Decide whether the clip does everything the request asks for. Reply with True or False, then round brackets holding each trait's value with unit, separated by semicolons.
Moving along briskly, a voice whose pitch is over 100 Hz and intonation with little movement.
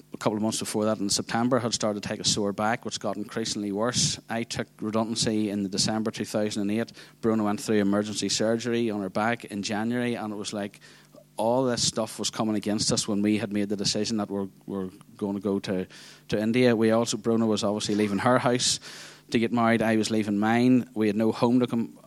True (235 wpm; 110 Hz; 2.0 semitones)